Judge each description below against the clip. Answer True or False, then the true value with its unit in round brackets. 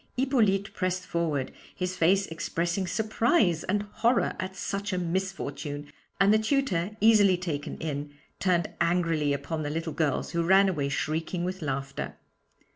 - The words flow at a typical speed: True (145 wpm)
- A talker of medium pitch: True (180 Hz)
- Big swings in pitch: False (3.8 semitones)